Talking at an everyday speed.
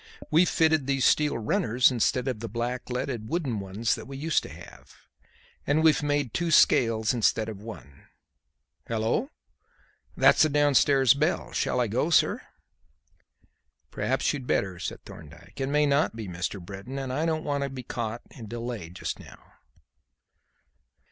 Yes: average, 155 wpm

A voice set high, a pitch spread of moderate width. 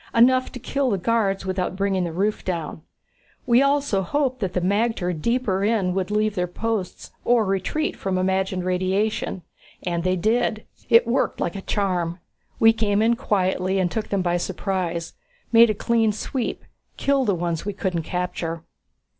Yes: high, 195 Hz; average, 3.9 semitones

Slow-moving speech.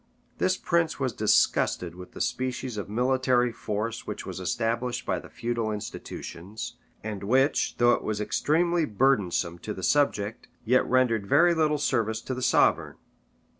No: average, 155 wpm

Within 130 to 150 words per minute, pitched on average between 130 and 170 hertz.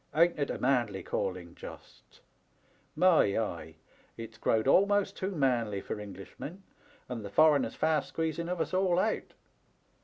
Yes: average, 145 wpm; medium, 140 Hz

